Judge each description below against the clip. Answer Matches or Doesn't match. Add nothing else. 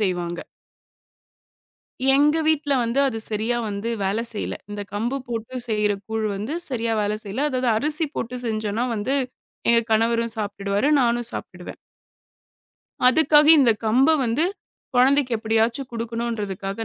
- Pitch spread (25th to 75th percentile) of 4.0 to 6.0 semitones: Doesn't match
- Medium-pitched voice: Doesn't match